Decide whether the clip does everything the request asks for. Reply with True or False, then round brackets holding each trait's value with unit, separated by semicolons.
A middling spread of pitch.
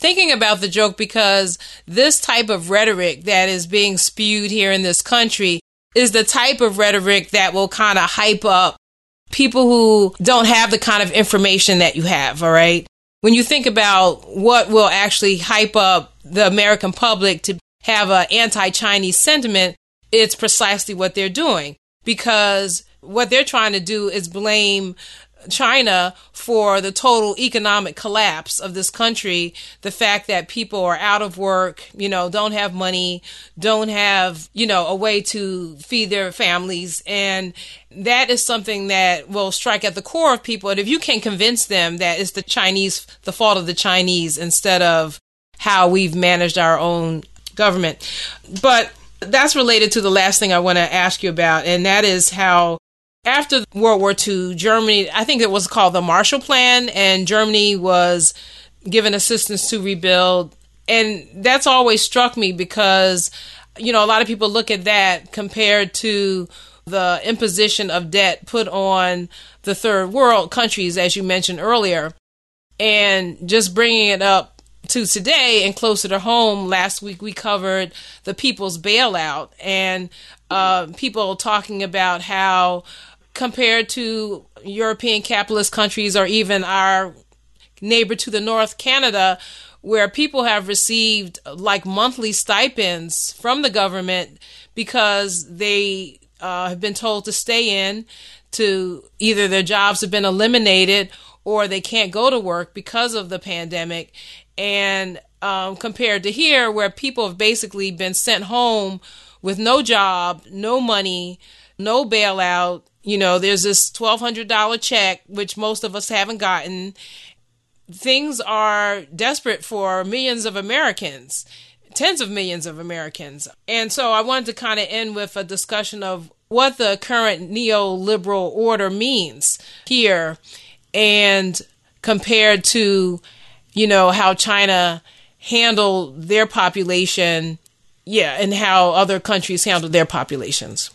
True (3.1 semitones)